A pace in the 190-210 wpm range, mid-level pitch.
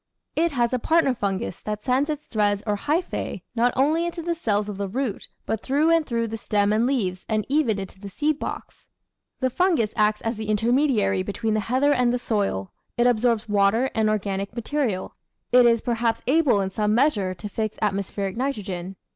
No: average, 195 wpm; high, 225 Hz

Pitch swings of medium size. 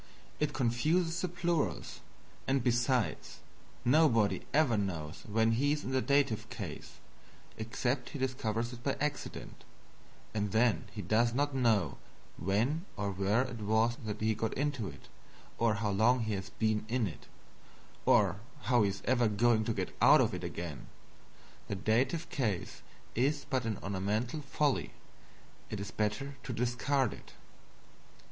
Yes: average, 4.1 semitones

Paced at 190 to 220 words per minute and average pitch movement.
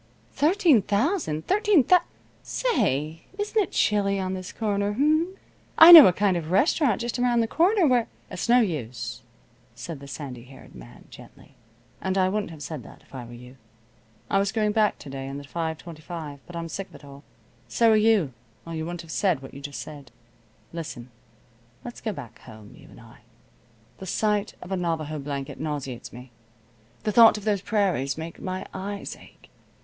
No: average, 195 wpm; wide, 7.3 semitones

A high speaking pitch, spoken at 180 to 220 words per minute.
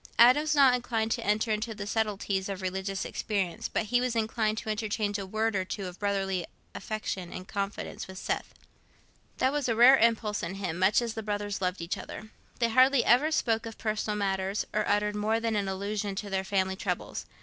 Yes: high, 210 Hz; fast, 205 wpm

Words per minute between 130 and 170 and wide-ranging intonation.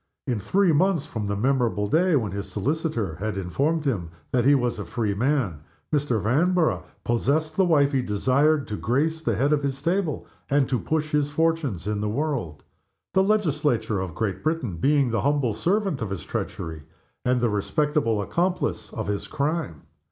No: average, 180 wpm; wide, 6.7 semitones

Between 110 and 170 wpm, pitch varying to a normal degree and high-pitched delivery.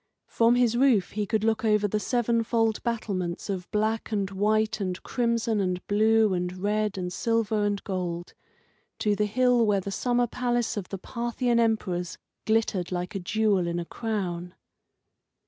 Yes: average, 165 wpm; average, 3.3 semitones; high, 210 Hz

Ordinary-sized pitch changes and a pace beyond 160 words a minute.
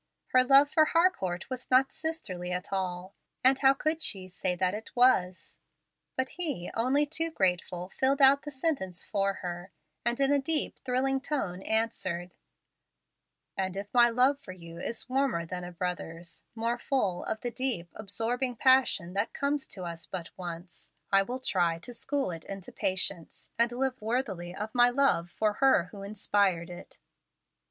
No: wide, 6.7 semitones; average, 170 wpm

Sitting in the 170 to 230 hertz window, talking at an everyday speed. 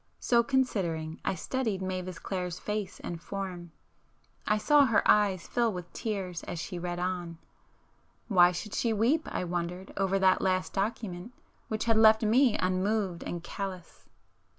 Yes: high, 190 Hz; average, 145 wpm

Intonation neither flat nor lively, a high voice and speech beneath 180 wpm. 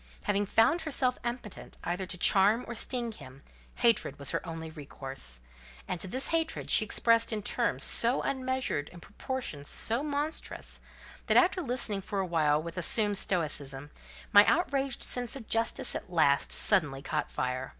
No: wide, 8.4 semitones; high, 205 Hz; average, 160 wpm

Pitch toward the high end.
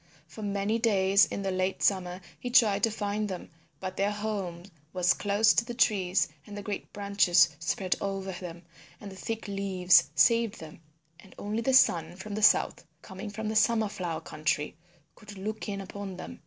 Yes: high, 200 Hz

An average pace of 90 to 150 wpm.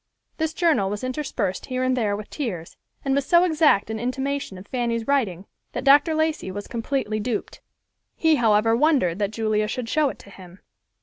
No: average, 185 wpm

